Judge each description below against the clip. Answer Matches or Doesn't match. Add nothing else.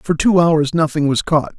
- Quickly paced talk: Matches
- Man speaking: Matches